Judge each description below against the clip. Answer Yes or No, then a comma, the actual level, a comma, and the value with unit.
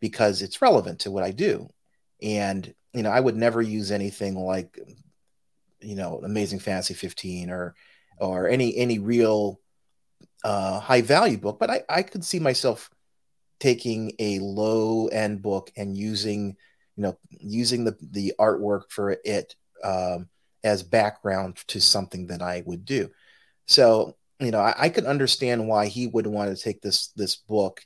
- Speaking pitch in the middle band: No, low, 105 Hz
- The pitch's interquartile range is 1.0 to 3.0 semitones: Yes, narrow, 2.5 semitones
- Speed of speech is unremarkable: Yes, average, 165 wpm